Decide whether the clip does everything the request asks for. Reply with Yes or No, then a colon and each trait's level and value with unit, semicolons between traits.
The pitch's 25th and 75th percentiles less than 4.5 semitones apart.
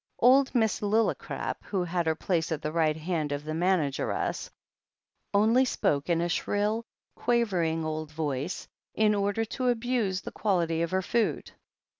No: wide, 5.4 semitones